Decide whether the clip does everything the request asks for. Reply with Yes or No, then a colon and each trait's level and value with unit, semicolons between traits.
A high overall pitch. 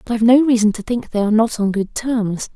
Yes: high, 225 Hz